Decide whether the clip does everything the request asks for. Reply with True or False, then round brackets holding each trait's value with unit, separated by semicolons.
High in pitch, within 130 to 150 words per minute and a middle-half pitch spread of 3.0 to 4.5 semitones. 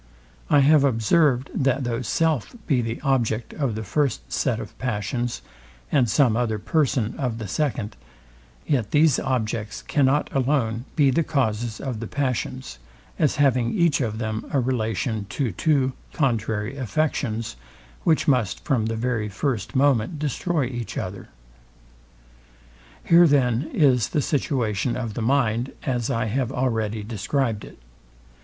False (125 Hz; 145 wpm; 4.0 semitones)